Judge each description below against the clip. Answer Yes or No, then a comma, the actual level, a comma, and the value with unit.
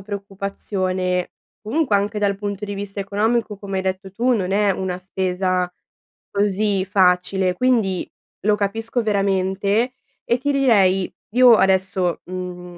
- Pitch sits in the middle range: No, high, 195 Hz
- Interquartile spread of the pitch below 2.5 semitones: Yes, narrow, 2.0 semitones